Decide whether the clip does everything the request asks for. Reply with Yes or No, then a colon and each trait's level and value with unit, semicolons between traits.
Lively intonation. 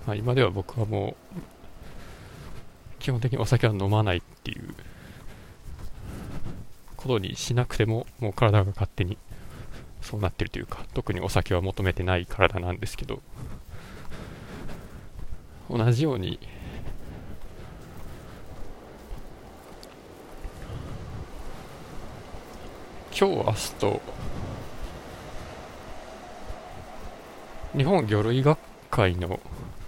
No: average, 4.2 semitones